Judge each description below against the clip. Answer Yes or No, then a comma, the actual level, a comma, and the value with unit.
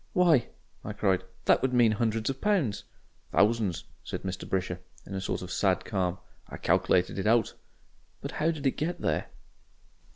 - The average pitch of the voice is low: Yes, low, 110 Hz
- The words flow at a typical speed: Yes, average, 170 wpm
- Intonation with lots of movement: Yes, wide, 5.9 semitones